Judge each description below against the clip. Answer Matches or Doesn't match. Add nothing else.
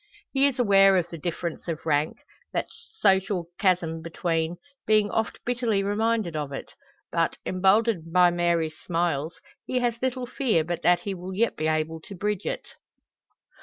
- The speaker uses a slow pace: Doesn't match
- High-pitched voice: Doesn't match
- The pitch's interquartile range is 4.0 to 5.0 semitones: Matches